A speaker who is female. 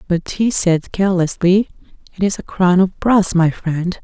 Yes: female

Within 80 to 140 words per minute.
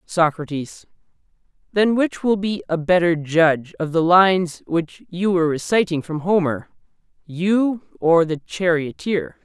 Yes: slow, 135 wpm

